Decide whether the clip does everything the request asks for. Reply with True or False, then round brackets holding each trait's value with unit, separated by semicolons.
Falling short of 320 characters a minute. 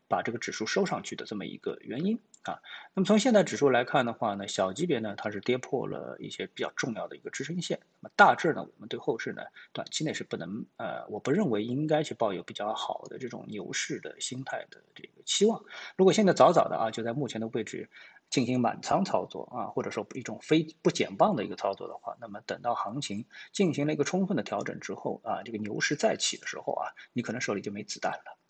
False (355 characters per minute)